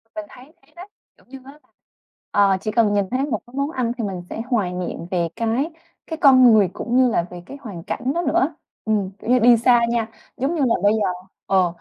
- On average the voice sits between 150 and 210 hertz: No, high, 235 Hz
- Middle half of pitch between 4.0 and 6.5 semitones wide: Yes, average, 4.7 semitones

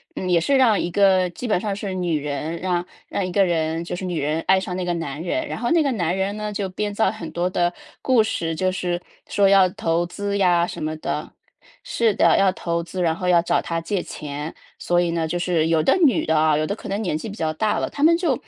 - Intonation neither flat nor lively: Yes, average, 3.4 semitones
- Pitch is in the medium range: Yes, medium, 180 Hz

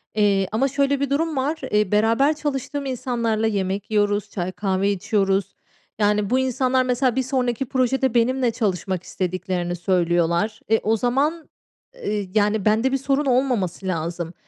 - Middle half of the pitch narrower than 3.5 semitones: No, average, 5.1 semitones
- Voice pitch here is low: No, high, 220 Hz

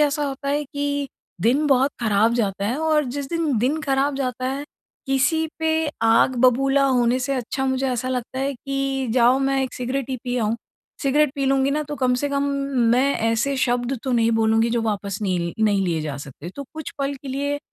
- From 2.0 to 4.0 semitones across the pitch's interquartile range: Yes, average, 3.0 semitones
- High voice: Yes, very high, 265 Hz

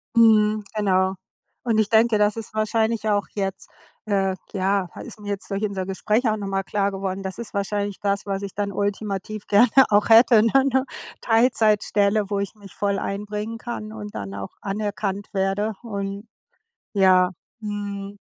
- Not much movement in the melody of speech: Yes, narrow, 1.6 semitones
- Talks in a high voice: Yes, high, 205 Hz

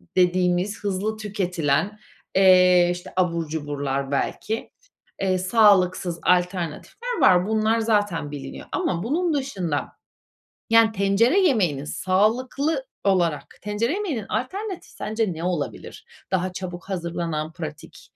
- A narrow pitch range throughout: No, average, 4.0 semitones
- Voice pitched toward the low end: No, medium, 185 Hz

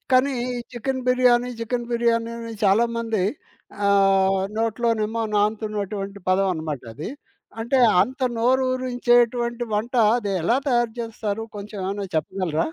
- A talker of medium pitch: No, high, 230 Hz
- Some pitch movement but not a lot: Yes, average, 3.1 semitones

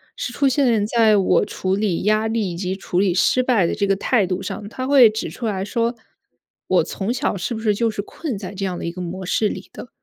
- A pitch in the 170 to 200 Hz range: No, high, 210 Hz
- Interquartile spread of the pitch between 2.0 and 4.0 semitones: Yes, average, 3.5 semitones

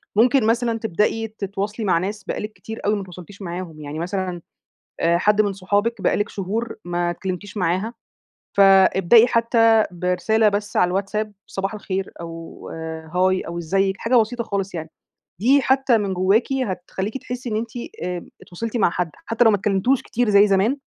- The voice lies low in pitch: No, high, 200 Hz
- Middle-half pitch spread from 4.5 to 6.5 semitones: No, average, 3.6 semitones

